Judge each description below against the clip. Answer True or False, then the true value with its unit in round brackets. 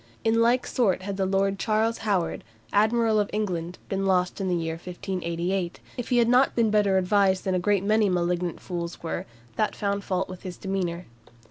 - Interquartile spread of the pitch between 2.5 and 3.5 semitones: True (2.9 semitones)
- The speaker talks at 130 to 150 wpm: False (195 wpm)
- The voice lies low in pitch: False (195 Hz)